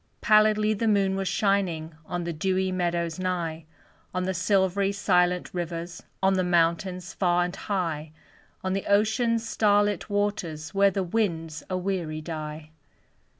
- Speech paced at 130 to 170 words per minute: Yes, average, 150 wpm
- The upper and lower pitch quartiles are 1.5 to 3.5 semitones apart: Yes, average, 2.9 semitones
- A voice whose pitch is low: No, medium, 185 Hz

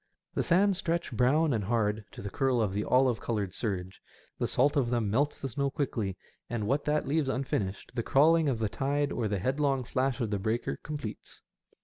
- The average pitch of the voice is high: No, low, 125 Hz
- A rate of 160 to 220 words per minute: Yes, fast, 205 wpm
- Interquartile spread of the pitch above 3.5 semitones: Yes, average, 4.9 semitones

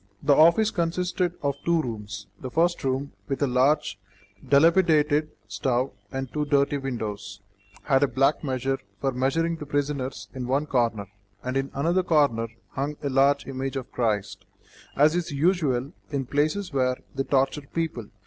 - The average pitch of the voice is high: No, medium, 140 Hz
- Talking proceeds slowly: No, average, 160 wpm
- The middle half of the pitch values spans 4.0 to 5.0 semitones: No, average, 3.0 semitones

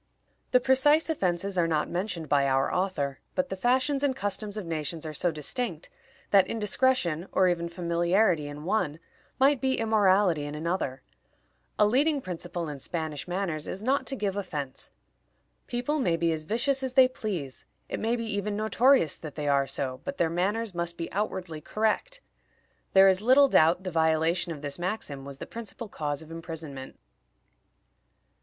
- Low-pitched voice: No, medium, 185 Hz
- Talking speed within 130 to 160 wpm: No, average, 170 wpm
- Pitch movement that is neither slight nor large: No, wide, 6.1 semitones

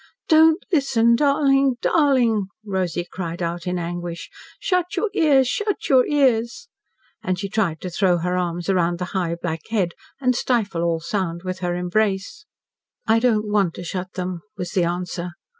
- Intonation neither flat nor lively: No, wide, 6.3 semitones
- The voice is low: No, high, 190 Hz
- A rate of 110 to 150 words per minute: No, average, 165 wpm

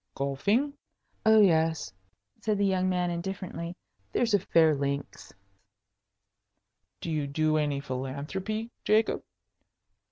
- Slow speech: Yes, slow, 105 wpm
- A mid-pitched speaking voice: Yes, medium, 170 Hz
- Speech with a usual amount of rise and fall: No, wide, 5.7 semitones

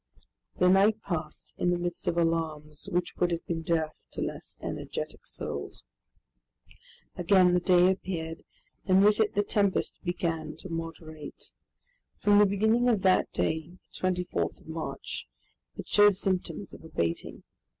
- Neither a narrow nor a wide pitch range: Yes, average, 3.0 semitones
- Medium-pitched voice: Yes, medium, 175 Hz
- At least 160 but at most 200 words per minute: No, average, 150 wpm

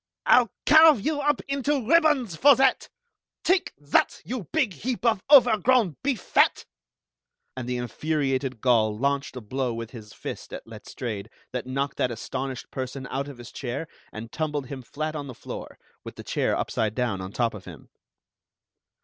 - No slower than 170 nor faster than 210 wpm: Yes, average, 175 wpm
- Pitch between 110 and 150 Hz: Yes, medium, 140 Hz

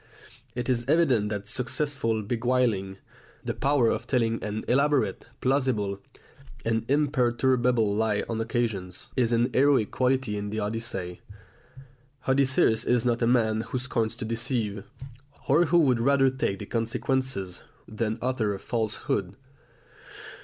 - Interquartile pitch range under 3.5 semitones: Yes, average, 3.1 semitones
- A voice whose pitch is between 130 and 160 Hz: No, low, 120 Hz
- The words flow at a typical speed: No, slow, 130 wpm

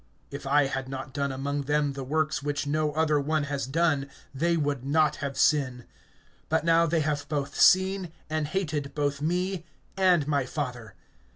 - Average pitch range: No, narrow, 2.2 semitones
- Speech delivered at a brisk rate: No, average, 175 wpm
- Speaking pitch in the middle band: Yes, medium, 145 Hz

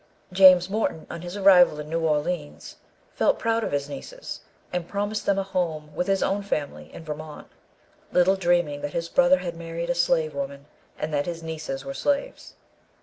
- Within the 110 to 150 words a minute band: No, average, 185 wpm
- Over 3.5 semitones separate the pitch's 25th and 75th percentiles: Yes, average, 4.2 semitones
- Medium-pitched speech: Yes, medium, 170 Hz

